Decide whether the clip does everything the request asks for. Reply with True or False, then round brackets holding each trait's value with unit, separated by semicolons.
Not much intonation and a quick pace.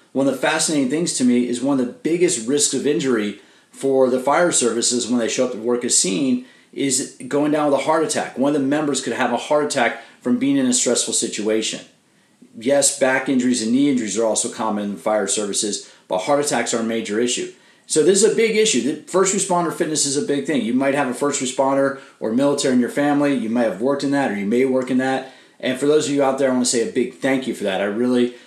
False (3.6 semitones; 260 wpm)